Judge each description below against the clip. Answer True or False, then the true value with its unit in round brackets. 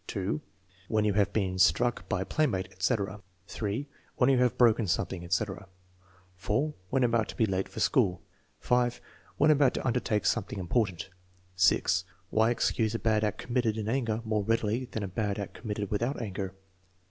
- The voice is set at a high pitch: False (110 Hz)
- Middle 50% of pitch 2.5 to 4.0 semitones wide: True (3.7 semitones)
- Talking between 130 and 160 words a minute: False (175 wpm)